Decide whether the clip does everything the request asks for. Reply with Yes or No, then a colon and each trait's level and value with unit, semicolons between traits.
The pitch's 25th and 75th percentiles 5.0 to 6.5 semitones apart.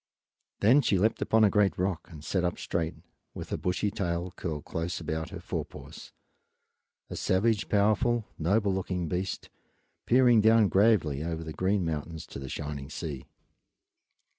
No: average, 4.4 semitones